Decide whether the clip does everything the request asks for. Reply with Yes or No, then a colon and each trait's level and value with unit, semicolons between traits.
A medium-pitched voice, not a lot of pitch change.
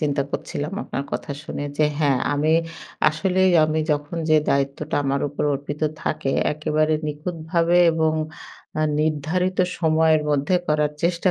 Yes: medium, 155 Hz; narrow, 1.8 semitones